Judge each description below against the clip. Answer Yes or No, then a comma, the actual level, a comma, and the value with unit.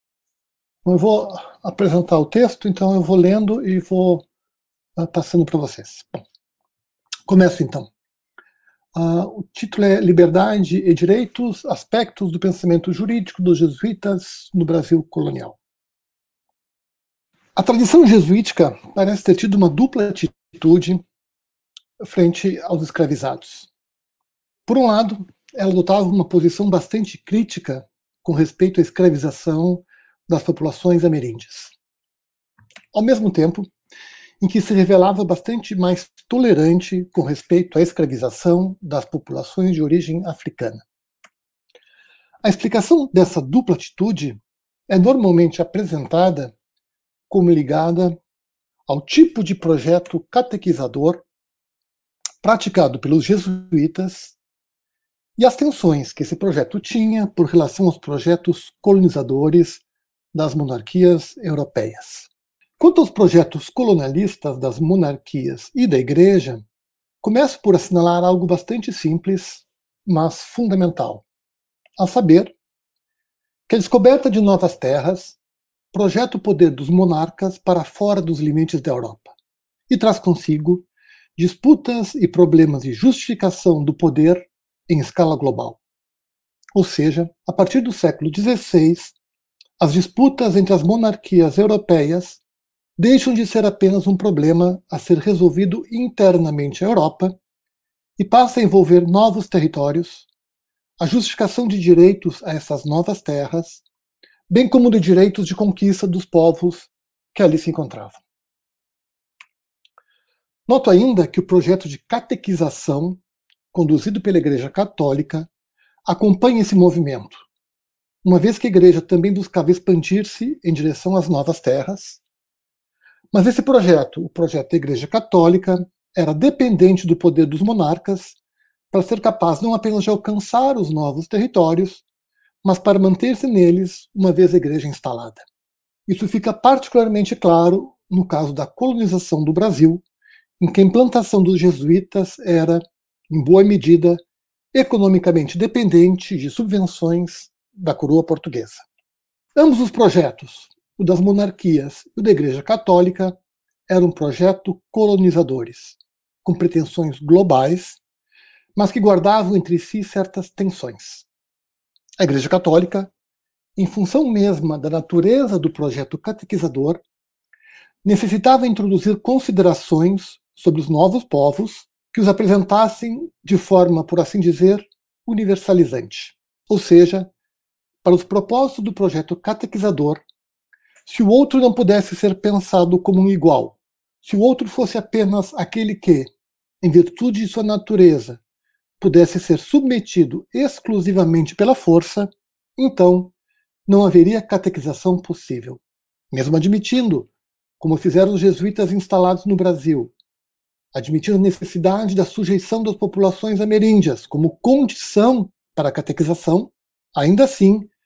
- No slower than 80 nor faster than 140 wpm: Yes, slow, 120 wpm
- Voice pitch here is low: No, medium, 185 Hz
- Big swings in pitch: No, average, 3.9 semitones